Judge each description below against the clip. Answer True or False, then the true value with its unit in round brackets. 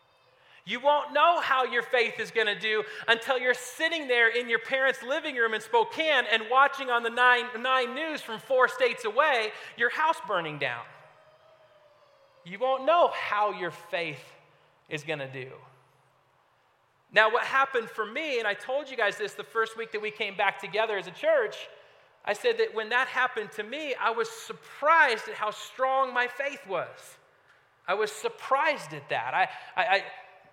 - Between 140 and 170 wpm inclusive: False (180 wpm)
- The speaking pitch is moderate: False (245 Hz)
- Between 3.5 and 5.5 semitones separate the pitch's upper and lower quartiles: True (5.0 semitones)